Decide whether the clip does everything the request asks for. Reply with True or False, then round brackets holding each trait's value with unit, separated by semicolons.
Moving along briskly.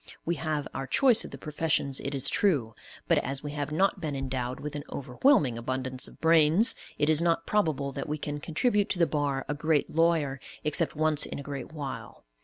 True (210 wpm)